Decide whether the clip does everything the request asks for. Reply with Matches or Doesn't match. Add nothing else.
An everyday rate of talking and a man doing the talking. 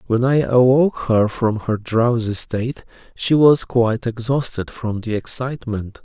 Matches